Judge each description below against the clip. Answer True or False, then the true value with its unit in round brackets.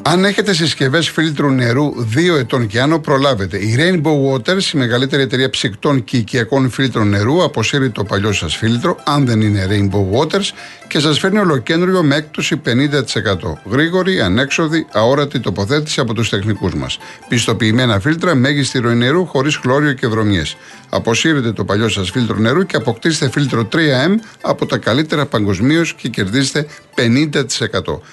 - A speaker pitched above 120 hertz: True (135 Hz)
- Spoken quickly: False (155 wpm)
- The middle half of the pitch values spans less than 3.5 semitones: False (5.3 semitones)